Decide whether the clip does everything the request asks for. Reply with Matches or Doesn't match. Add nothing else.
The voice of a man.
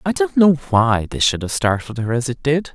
Matches